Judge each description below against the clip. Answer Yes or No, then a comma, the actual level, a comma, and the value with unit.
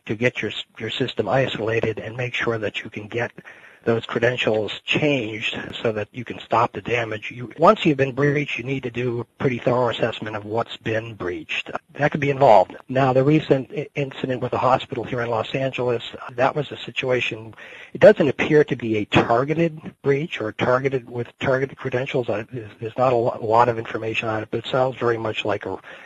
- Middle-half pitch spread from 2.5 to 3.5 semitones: Yes, average, 3.2 semitones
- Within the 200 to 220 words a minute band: Yes, fast, 205 wpm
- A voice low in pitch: Yes, low, 120 Hz